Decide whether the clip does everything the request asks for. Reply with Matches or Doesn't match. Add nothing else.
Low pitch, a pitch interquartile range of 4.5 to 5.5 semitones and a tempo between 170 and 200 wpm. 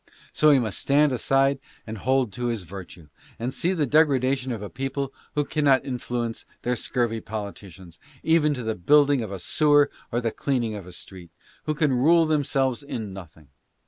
Matches